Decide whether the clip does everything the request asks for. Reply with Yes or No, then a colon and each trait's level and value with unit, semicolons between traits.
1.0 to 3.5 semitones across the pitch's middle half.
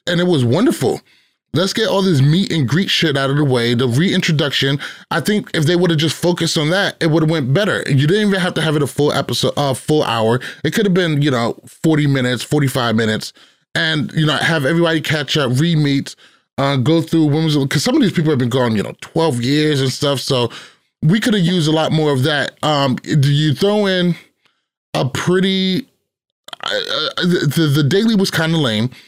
No: average, 4.1 semitones